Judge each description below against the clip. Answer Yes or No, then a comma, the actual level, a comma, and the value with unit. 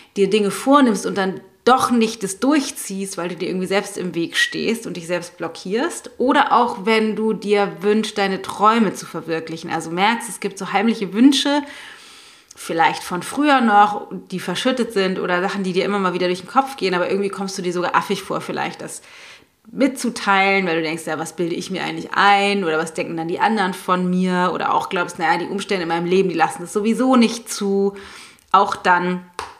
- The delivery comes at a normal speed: No, fast, 210 wpm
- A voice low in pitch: No, high, 195 Hz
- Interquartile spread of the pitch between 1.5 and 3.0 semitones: No, average, 3.6 semitones